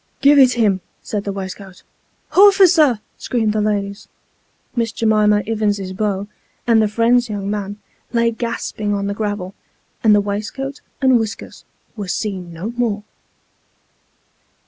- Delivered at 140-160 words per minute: Yes, average, 145 wpm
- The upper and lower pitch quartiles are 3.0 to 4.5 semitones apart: No, narrow, 2.5 semitones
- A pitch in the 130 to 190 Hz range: No, high, 210 Hz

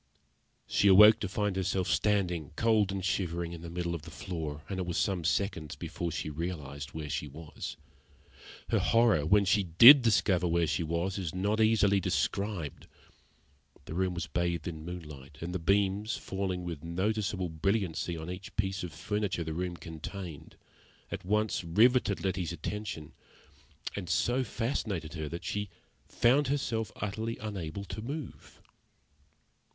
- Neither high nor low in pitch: No, very low, 90 Hz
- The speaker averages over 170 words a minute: No, average, 155 wpm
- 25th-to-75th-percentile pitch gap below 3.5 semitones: No, average, 3.8 semitones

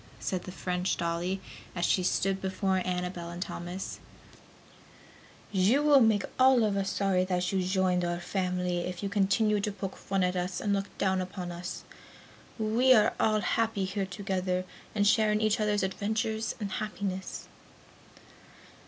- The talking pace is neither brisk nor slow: Yes, average, 160 wpm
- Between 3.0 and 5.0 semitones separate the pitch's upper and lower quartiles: No, narrow, 2.5 semitones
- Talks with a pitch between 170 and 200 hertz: Yes, high, 190 Hz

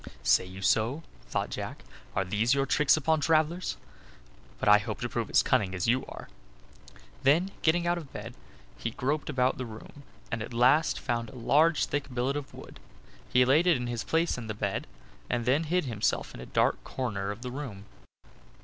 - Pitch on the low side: Yes, low, 125 Hz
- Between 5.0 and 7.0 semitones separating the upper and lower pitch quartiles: Yes, average, 5.3 semitones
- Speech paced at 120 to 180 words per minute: No, average, 200 wpm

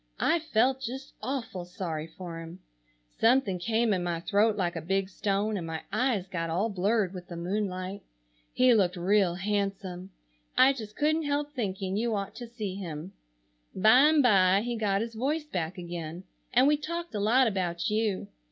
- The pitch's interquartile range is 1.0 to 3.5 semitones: No, average, 4.8 semitones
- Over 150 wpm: Yes, average, 170 wpm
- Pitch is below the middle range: No, high, 200 Hz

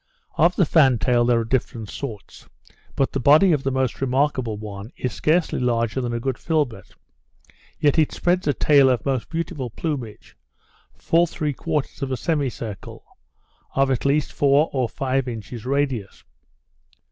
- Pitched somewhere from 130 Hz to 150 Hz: Yes, low, 135 Hz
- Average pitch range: Yes, average, 3.7 semitones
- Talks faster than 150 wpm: Yes, average, 165 wpm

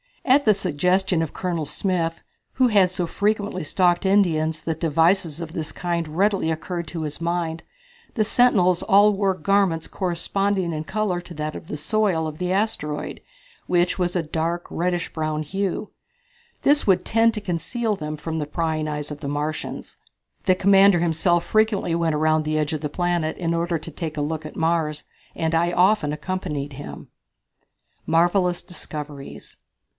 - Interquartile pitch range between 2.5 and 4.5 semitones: Yes, average, 3.4 semitones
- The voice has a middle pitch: Yes, medium, 170 Hz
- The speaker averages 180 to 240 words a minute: No, average, 170 wpm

